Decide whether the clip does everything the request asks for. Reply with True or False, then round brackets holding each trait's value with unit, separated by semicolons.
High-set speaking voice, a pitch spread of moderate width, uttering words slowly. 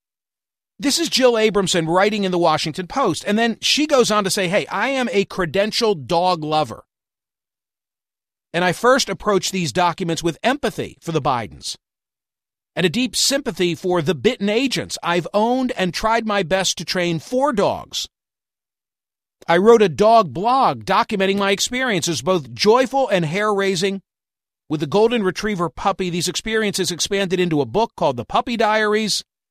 False (200 Hz; 4.0 semitones; 165 wpm)